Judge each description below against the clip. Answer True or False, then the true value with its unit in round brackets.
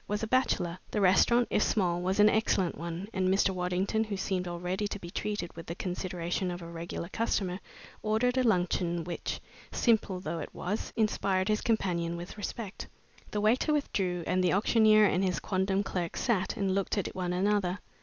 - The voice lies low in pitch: False (190 Hz)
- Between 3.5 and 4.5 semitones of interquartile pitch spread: False (3.0 semitones)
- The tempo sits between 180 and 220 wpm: True (185 wpm)